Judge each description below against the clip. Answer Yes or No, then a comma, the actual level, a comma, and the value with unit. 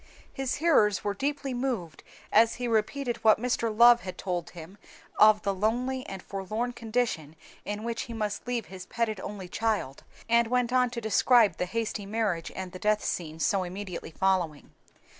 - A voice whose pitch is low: No, high, 215 Hz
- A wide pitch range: No, average, 4.1 semitones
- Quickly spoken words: No, average, 175 wpm